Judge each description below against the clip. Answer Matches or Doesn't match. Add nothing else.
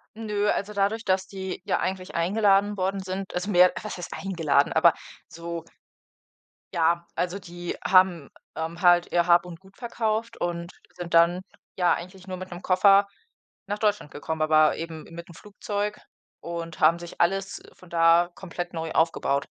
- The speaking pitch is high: Doesn't match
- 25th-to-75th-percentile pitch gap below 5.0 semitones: Matches